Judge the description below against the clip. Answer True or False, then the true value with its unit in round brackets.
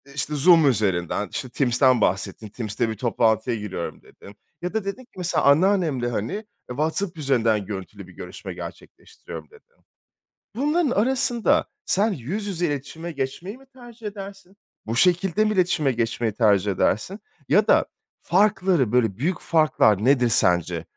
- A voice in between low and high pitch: True (145 Hz)